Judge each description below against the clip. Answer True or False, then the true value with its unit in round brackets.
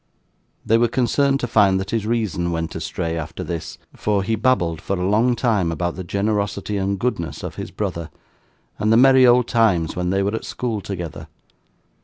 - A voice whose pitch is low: True (100 Hz)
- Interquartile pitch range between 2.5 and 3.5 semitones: False (4.7 semitones)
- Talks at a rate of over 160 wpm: True (190 wpm)